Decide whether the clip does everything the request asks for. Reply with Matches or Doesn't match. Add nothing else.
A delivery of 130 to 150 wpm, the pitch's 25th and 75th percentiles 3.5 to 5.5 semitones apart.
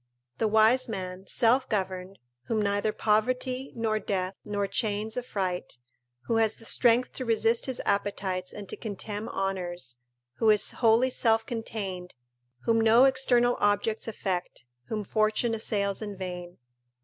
Doesn't match